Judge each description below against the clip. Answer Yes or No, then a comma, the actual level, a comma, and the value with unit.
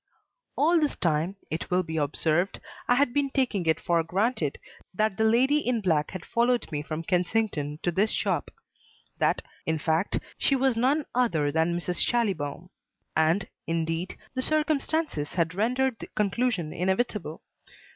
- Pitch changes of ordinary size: No, wide, 7.2 semitones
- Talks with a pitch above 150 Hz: Yes, high, 190 Hz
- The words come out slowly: No, average, 155 wpm